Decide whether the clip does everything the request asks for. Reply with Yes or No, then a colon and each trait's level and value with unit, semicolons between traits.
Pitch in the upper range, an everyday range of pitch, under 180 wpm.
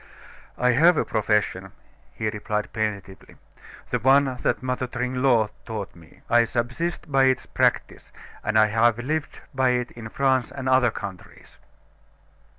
No: low, 120 Hz; average, 3.3 semitones; average, 145 wpm